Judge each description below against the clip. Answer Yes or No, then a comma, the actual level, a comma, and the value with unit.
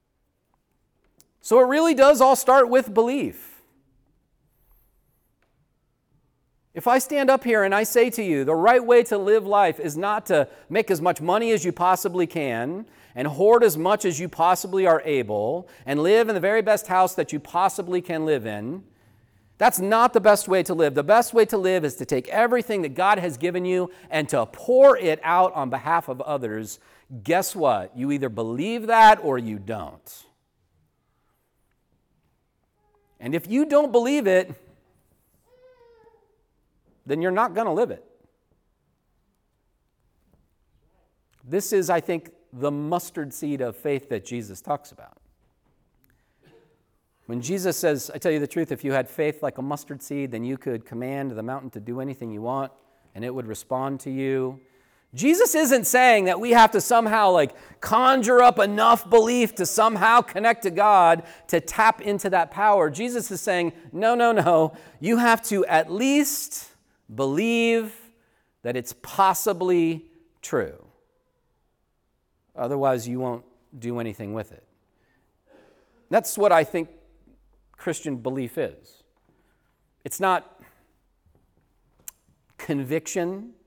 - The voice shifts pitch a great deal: Yes, wide, 8.5 semitones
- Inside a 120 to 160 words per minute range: Yes, average, 150 wpm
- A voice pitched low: No, medium, 175 Hz